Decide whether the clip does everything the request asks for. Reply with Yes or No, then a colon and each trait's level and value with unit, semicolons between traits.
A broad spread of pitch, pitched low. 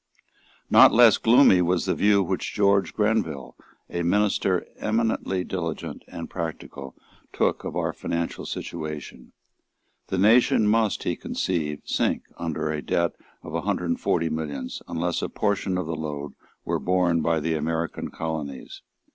No: average, 4.0 semitones; very low, 85 Hz